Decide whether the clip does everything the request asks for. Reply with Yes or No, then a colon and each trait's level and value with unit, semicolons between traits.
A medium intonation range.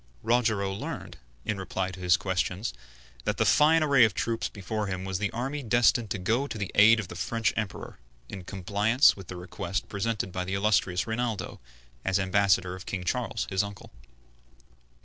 Yes: average, 3.3 semitones